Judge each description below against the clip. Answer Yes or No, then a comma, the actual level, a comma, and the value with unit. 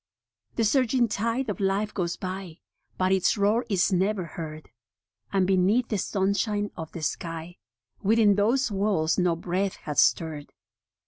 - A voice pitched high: Yes, high, 195 Hz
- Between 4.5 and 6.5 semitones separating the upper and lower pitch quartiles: No, average, 3.3 semitones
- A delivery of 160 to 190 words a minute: No, average, 145 wpm